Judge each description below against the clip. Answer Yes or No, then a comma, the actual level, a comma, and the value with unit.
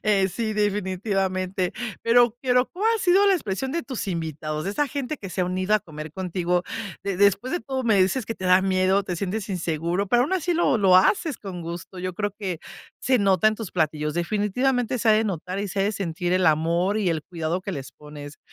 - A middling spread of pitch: Yes, average, 4.0 semitones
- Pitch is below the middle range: No, high, 195 Hz